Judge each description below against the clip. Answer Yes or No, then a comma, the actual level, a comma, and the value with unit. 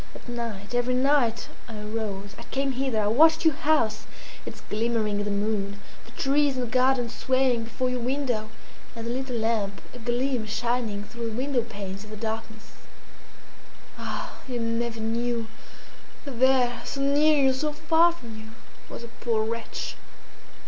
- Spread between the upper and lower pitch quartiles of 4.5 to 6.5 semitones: No, average, 3.0 semitones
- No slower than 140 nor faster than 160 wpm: No, average, 170 wpm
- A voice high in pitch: Yes, high, 235 Hz